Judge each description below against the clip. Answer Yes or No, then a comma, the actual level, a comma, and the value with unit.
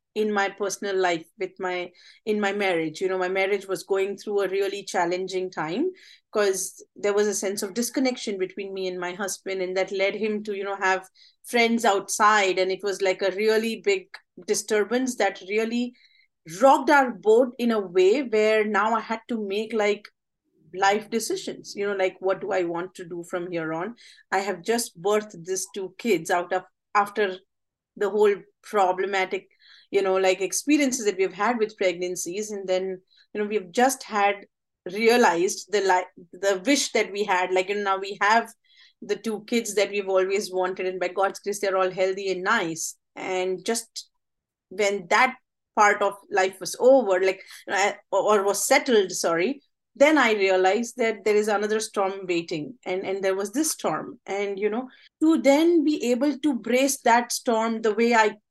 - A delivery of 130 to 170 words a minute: No, average, 190 wpm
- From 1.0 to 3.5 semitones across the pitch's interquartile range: Yes, average, 3.2 semitones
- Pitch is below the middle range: No, high, 200 Hz